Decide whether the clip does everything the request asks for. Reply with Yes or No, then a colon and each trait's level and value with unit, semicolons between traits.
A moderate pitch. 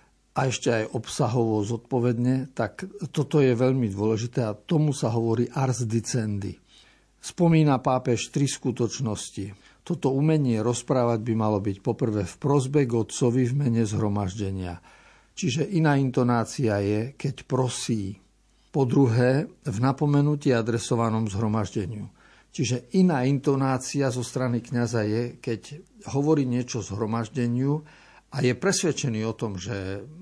No: low, 125 Hz